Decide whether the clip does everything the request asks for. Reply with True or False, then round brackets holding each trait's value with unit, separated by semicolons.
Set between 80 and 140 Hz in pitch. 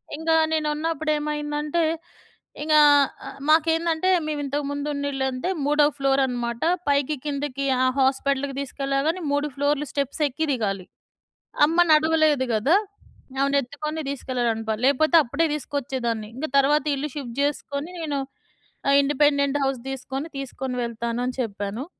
False (280 Hz)